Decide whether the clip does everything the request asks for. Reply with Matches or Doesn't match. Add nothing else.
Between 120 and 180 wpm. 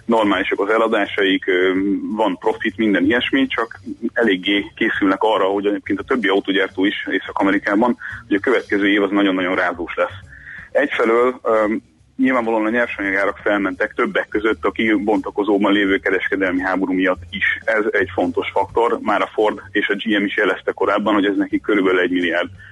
Matches